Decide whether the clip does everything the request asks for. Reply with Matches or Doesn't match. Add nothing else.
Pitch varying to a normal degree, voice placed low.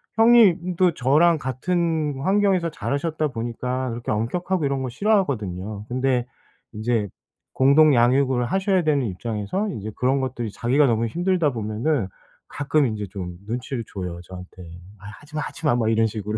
Doesn't match